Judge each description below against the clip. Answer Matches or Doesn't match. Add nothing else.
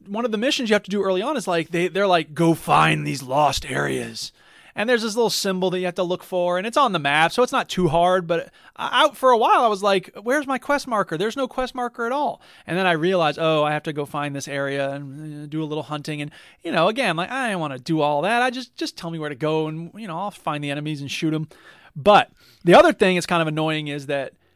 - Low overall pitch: Doesn't match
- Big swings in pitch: Matches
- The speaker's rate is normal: Doesn't match